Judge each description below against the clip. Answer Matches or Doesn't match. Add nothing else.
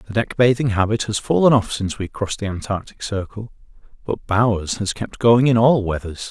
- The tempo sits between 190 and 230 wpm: Matches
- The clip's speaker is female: Doesn't match